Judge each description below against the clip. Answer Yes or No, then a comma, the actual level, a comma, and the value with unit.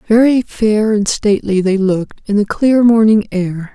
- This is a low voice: No, high, 210 Hz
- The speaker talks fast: No, average, 175 wpm